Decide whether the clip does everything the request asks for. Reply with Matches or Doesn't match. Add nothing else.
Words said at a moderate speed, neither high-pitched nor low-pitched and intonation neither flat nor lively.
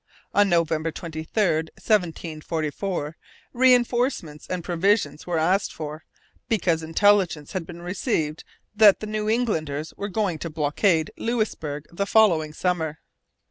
Doesn't match